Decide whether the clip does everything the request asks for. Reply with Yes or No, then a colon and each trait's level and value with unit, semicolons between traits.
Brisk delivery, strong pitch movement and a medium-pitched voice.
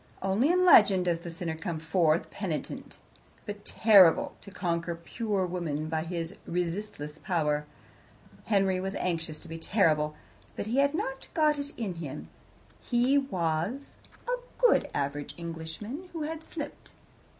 No: average, 140 wpm; wide, 6.1 semitones; medium, 180 Hz